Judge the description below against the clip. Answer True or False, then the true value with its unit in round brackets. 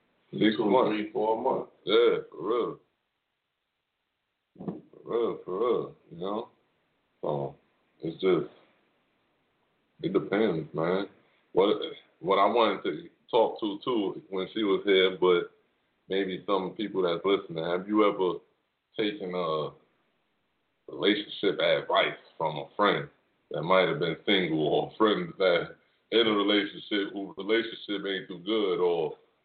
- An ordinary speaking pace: False (130 wpm)